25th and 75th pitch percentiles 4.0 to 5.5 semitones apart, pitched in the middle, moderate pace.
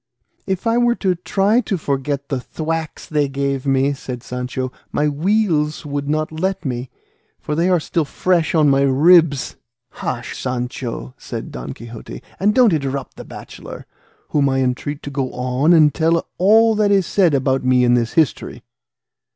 Yes: average, 4.7 semitones; medium, 145 Hz; average, 170 wpm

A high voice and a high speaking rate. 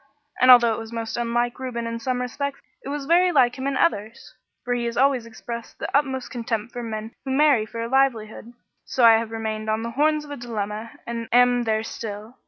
Yes: high, 235 Hz; fast, 220 wpm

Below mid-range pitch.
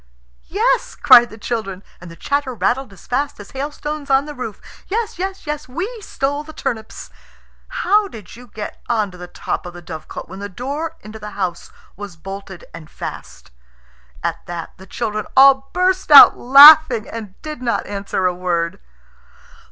No: high, 235 Hz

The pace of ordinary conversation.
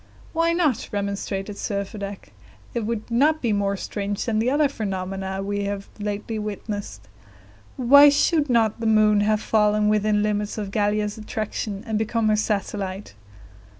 Yes: average, 155 wpm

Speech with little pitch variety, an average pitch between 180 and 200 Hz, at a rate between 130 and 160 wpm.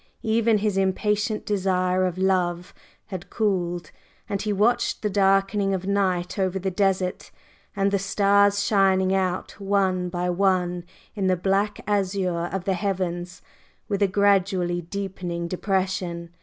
Yes: narrow, 1.8 semitones; high, 190 Hz; average, 140 wpm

